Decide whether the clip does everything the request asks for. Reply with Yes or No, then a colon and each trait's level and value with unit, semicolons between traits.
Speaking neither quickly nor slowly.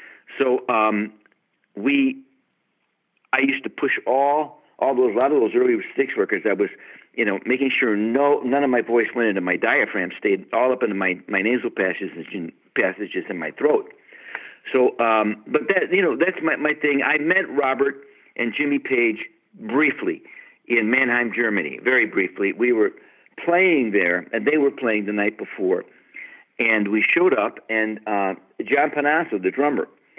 Yes: average, 170 wpm